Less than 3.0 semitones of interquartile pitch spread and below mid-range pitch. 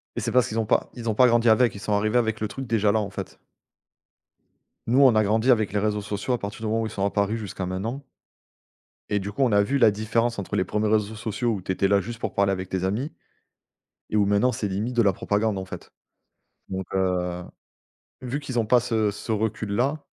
Yes: narrow, 2.6 semitones; low, 110 Hz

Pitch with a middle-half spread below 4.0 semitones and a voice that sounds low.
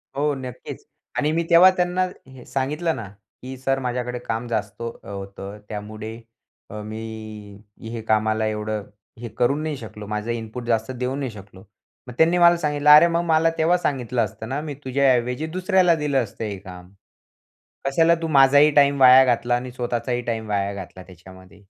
No: average, 5.3 semitones; low, 125 Hz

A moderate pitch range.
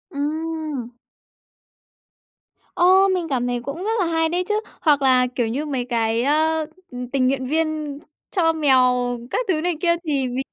Yes: average, 4.1 semitones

